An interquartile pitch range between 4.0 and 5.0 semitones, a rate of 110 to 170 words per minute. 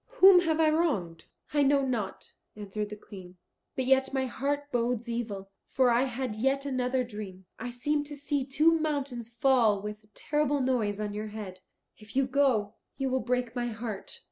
No: average, 4.6 semitones; average, 185 wpm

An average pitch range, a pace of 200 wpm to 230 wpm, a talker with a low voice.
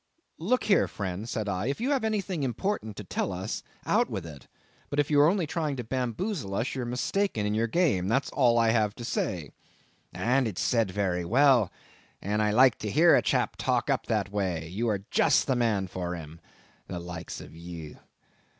No: wide, 6.5 semitones; fast, 205 wpm; low, 110 Hz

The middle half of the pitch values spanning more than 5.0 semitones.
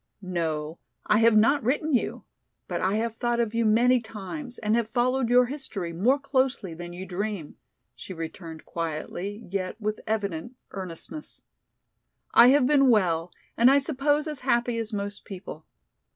Yes: wide, 5.4 semitones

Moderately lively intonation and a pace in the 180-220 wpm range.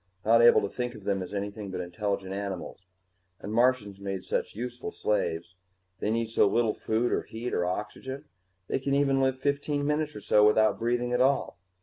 Yes: average, 4.3 semitones; average, 195 wpm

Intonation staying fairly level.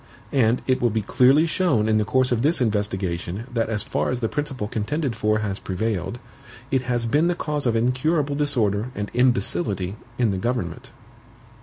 No: average, 4.1 semitones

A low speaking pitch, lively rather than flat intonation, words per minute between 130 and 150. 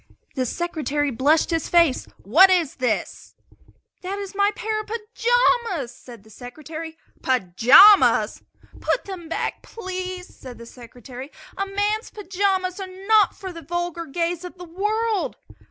No: very high, 350 Hz; wide, 5.7 semitones; average, 140 wpm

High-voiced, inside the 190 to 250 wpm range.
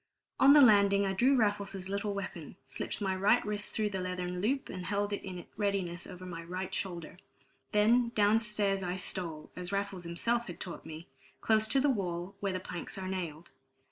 Yes: high, 195 Hz; average, 195 wpm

